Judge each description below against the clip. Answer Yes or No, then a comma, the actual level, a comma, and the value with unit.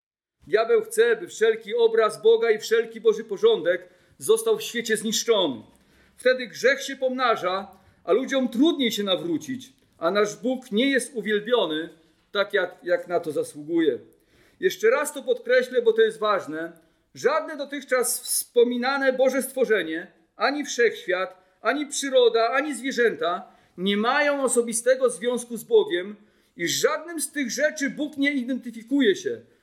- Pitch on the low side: No, very high, 255 Hz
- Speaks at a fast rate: No, average, 140 wpm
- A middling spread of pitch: No, wide, 5.8 semitones